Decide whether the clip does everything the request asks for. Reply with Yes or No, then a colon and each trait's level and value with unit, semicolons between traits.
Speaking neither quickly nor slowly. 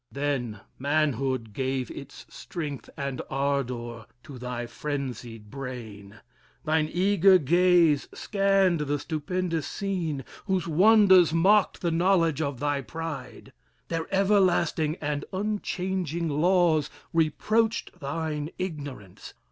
No: slow, 105 wpm